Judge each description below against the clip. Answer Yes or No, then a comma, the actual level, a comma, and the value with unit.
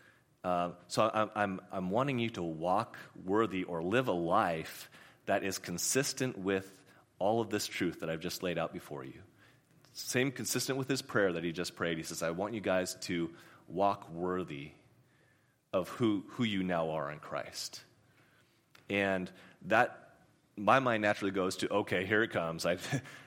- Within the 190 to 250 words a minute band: No, average, 175 wpm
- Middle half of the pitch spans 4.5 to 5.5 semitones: Yes, average, 4.8 semitones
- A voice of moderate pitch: No, very low, 95 Hz